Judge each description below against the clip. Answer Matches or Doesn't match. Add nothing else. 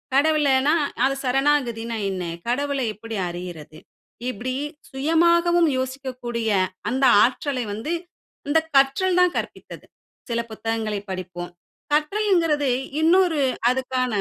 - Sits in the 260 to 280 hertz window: Matches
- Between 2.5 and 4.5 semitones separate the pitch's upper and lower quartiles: Doesn't match